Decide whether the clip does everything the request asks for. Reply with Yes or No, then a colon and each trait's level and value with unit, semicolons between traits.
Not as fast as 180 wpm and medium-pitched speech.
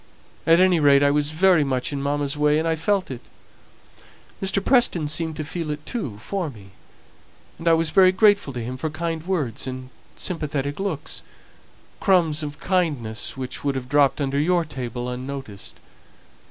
Yes: average, 170 wpm; medium, 150 Hz